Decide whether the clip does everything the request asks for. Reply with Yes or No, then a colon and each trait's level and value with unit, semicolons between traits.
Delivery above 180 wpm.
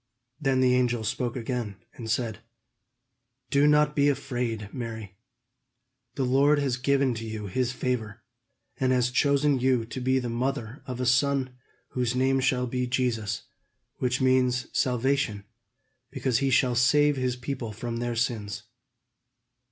No: average, 145 wpm